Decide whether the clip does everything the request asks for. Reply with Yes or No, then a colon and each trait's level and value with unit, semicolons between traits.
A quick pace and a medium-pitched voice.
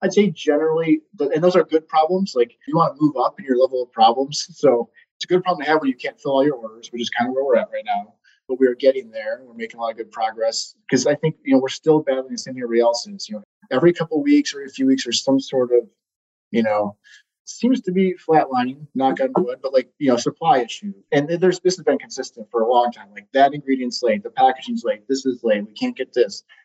Yes: fast, 265 wpm; medium, 150 Hz